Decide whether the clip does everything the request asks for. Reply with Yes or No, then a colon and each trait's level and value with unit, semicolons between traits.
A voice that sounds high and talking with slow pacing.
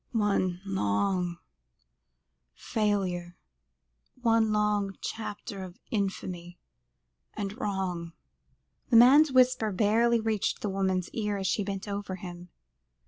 Yes: high, 200 Hz; slow, 105 wpm